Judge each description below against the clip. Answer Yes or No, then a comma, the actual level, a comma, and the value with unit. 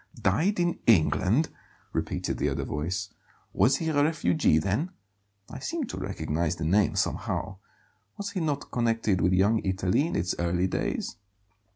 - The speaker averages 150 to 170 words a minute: Yes, average, 155 wpm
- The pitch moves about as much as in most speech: No, wide, 8.8 semitones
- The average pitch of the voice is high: No, low, 100 Hz